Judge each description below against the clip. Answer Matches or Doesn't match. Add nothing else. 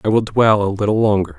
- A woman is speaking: Doesn't match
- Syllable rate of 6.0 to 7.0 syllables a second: Matches